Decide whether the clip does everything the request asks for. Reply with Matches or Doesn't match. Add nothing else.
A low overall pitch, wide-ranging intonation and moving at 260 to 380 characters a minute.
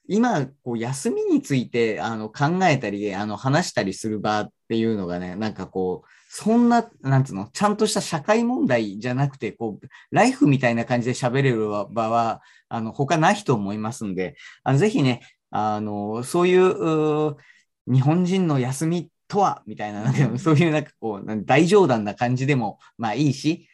Matches